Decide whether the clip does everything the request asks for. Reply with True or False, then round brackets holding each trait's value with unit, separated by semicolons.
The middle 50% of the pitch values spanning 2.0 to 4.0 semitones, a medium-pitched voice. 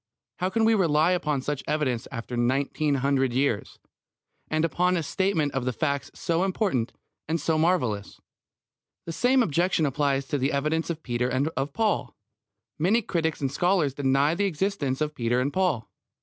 False (4.7 semitones; 150 Hz)